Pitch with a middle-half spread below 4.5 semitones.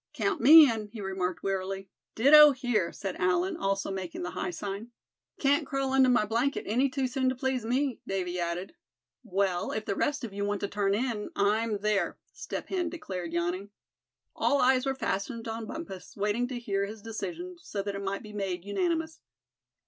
No: average, 5.2 semitones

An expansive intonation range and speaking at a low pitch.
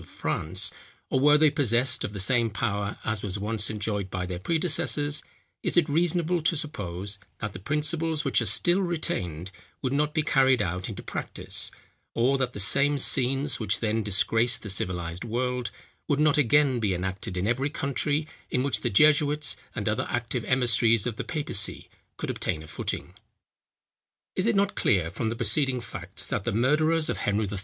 Yes: wide, 6.4 semitones; low, 125 Hz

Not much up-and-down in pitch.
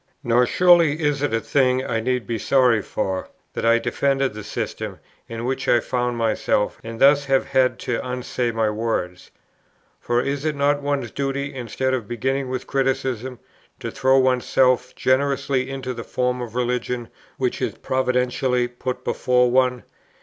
Yes: narrow, 2.0 semitones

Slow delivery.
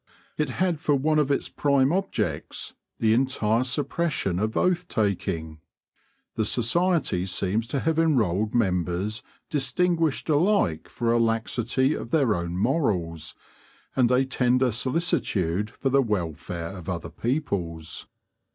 Yes: slow, 130 wpm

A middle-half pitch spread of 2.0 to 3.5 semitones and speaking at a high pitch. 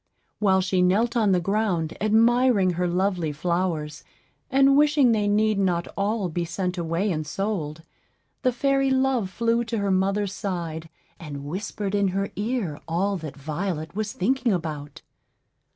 No: average, 4.3 semitones; high, 195 Hz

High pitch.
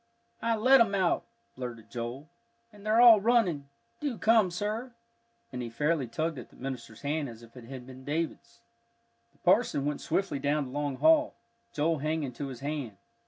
No: medium, 150 Hz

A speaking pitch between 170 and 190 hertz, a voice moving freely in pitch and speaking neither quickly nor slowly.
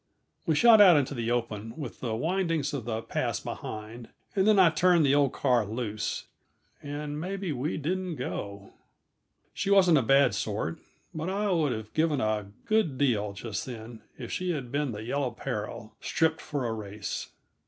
No: low, 135 Hz; wide, 6.5 semitones; average, 175 wpm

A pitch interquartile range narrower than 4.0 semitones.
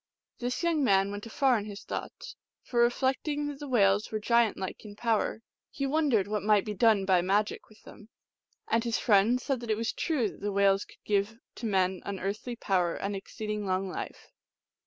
Yes: average, 3.4 semitones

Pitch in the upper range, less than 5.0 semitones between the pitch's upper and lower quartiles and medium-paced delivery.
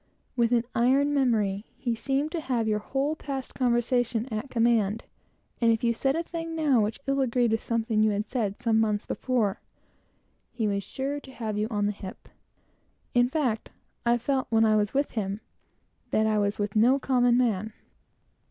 Yes: high, 235 Hz; average, 3.5 semitones; average, 170 wpm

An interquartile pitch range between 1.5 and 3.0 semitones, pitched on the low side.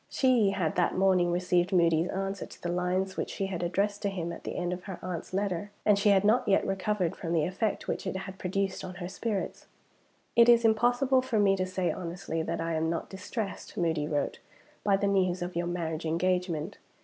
No: narrow, 2.4 semitones; medium, 185 Hz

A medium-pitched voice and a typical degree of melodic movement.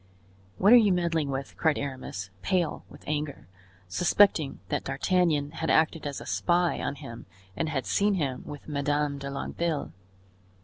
Yes: medium, 150 Hz; average, 3.7 semitones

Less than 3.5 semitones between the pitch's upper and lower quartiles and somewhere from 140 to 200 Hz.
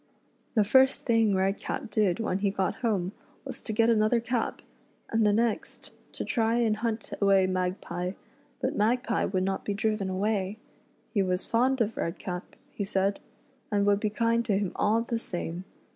No: average, 3.0 semitones; high, 210 Hz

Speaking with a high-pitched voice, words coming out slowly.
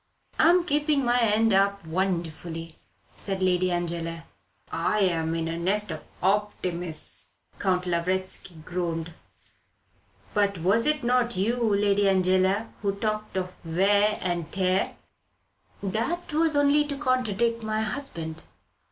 Yes: high, 195 Hz; slow, 125 wpm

